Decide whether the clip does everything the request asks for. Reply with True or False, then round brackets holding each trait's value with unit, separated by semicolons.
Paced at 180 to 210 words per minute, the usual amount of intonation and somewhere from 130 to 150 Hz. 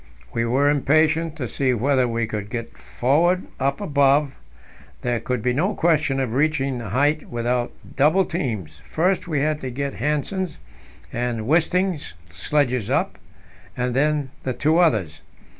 False (150 wpm; 4.1 semitones; 140 Hz)